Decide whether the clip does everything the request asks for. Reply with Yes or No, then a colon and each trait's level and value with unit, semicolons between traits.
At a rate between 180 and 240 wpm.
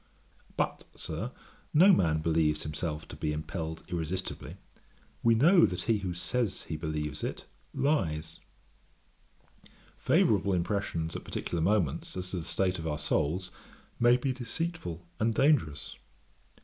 No: slow, 135 wpm